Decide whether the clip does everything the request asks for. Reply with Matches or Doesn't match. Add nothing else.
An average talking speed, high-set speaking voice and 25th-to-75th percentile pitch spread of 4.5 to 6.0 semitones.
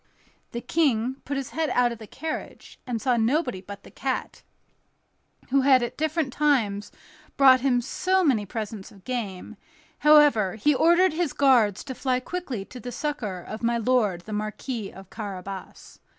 Matches